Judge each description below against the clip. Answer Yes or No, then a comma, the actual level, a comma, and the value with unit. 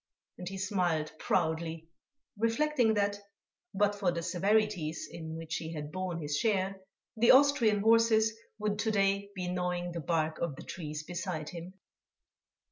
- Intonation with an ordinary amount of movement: Yes, average, 4.3 semitones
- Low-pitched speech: No, medium, 185 Hz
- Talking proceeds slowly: No, average, 150 wpm